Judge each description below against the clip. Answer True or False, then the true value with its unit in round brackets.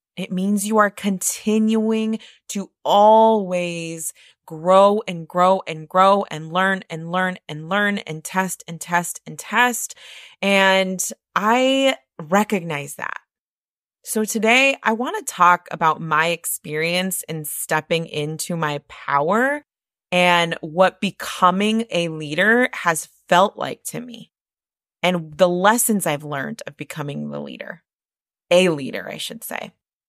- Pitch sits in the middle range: True (180 Hz)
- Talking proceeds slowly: True (130 wpm)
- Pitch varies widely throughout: False (4.4 semitones)